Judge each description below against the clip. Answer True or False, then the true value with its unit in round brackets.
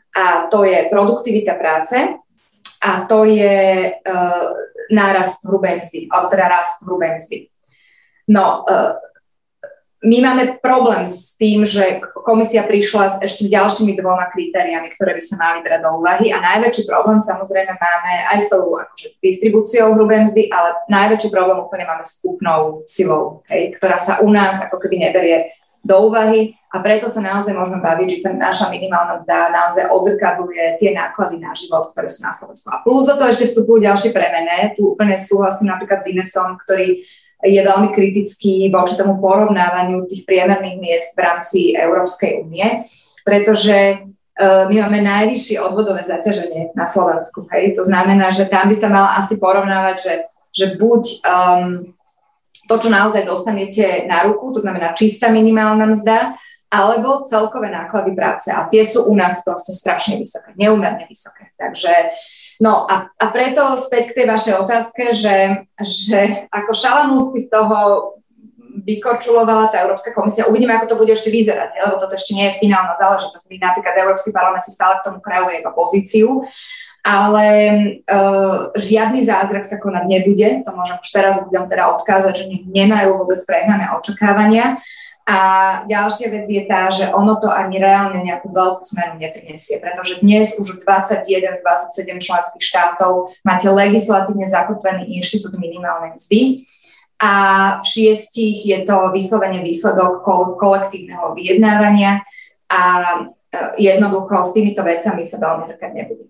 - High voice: True (195 Hz)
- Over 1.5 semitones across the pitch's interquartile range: True (2.8 semitones)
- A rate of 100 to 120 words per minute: False (155 wpm)